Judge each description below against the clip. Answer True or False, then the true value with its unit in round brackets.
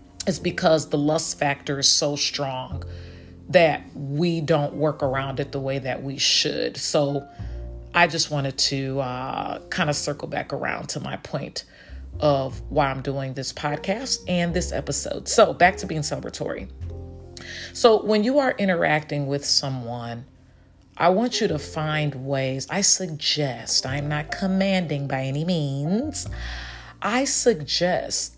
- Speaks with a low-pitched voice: False (145 Hz)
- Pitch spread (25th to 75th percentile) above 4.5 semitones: False (4.2 semitones)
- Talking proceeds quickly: False (150 wpm)